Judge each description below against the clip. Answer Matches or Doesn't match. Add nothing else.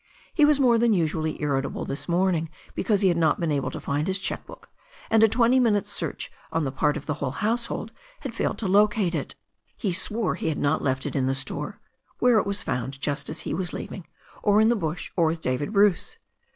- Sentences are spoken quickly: Matches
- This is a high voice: Doesn't match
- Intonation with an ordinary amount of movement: Doesn't match